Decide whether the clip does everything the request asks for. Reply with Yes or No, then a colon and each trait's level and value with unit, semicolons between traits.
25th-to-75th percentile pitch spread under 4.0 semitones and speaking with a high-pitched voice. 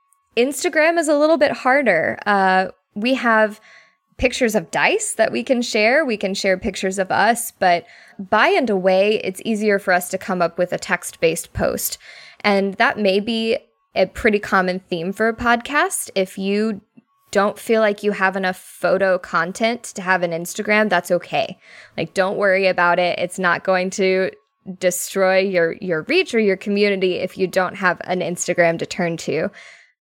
Yes: average, 3.6 semitones; high, 195 Hz